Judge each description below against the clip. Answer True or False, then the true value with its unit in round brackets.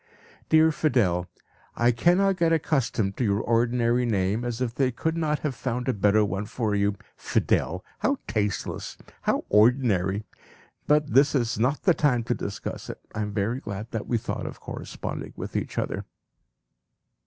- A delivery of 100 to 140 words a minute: False (165 wpm)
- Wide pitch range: False (4.9 semitones)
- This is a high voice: False (120 Hz)